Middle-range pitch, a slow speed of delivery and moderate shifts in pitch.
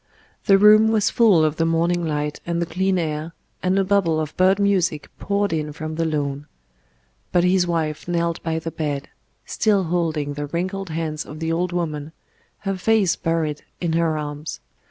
No: medium, 165 Hz; average, 180 wpm; average, 3.2 semitones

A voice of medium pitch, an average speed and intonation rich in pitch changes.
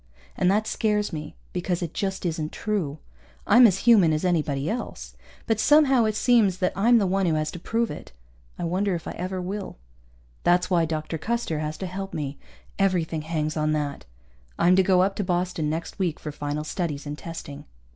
No: medium, 180 Hz; average, 195 wpm; average, 4.2 semitones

